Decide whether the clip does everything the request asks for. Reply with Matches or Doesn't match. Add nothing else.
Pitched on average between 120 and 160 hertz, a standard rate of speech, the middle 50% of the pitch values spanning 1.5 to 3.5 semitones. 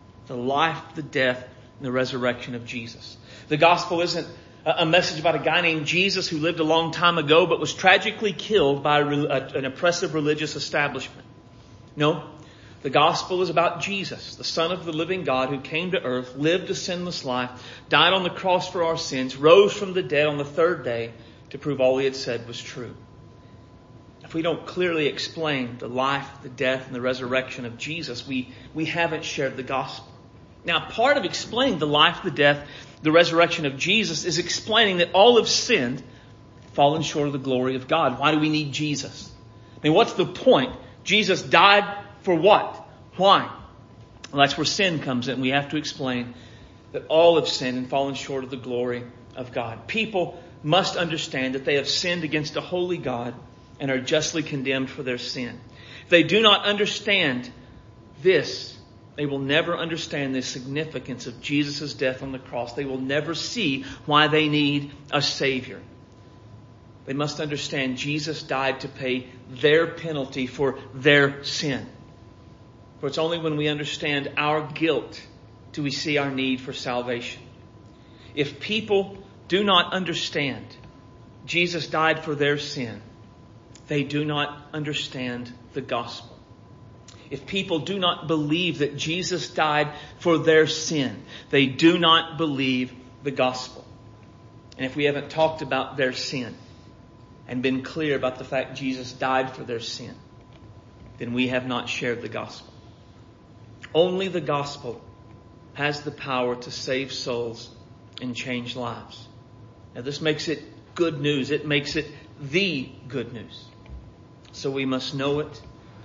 Doesn't match